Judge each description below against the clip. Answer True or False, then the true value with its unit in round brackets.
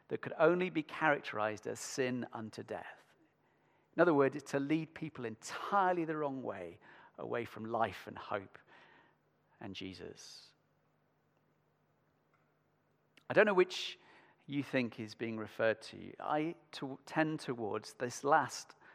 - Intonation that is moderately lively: False (5.7 semitones)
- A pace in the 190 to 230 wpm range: False (135 wpm)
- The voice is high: False (135 Hz)